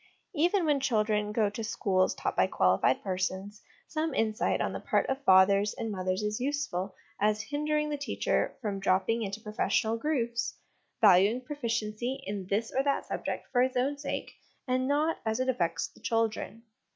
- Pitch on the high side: Yes, high, 225 Hz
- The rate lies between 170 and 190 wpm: Yes, average, 175 wpm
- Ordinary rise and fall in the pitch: Yes, average, 4.9 semitones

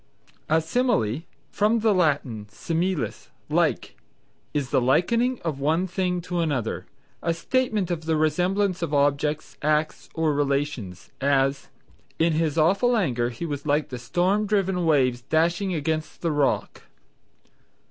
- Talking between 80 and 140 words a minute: Yes, slow, 135 wpm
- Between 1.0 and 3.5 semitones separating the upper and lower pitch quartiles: No, average, 4.2 semitones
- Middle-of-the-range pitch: Yes, medium, 160 Hz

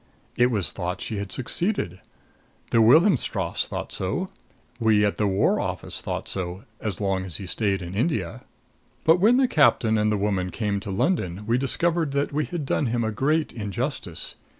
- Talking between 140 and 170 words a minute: No, average, 185 wpm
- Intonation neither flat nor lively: No, wide, 6.8 semitones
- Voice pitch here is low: Yes, low, 110 Hz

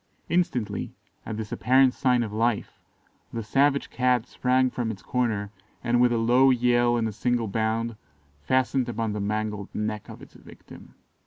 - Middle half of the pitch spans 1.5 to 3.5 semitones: Yes, narrow, 2.5 semitones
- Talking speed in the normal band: Yes, average, 165 wpm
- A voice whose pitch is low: Yes, low, 120 Hz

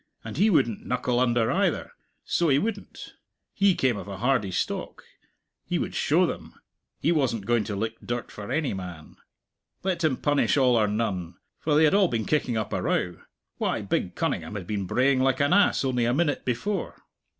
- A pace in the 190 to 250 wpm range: Yes, average, 195 wpm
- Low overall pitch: Yes, low, 125 Hz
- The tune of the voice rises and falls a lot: Yes, wide, 5.8 semitones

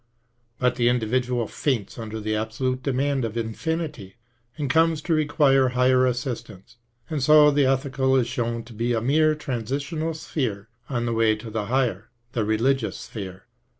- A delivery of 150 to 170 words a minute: Yes, average, 160 wpm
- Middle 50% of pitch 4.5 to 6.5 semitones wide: No, average, 3.7 semitones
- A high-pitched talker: No, low, 125 Hz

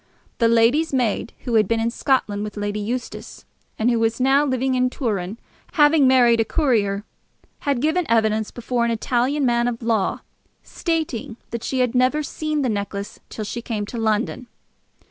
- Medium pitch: No, high, 235 Hz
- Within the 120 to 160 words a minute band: No, average, 175 wpm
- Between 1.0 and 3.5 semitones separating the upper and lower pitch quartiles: Yes, average, 3.1 semitones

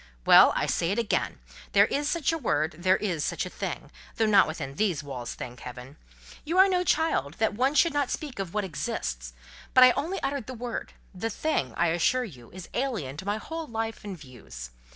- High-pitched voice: Yes, high, 205 Hz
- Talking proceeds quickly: Yes, fast, 210 wpm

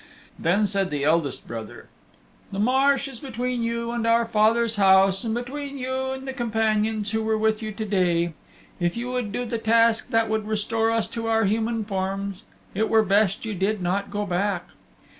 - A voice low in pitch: No, high, 220 Hz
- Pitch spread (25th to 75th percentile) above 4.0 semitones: No, average, 2.8 semitones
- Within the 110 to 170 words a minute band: No, average, 190 wpm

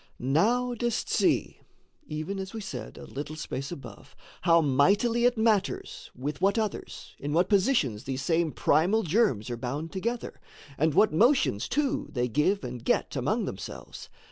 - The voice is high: No, medium, 170 Hz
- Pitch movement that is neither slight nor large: No, wide, 8.1 semitones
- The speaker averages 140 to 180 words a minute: Yes, average, 160 wpm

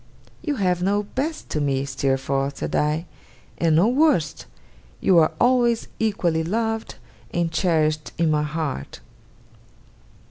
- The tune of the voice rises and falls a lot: Yes, wide, 6.7 semitones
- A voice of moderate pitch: Yes, medium, 165 Hz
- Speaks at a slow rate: Yes, slow, 130 wpm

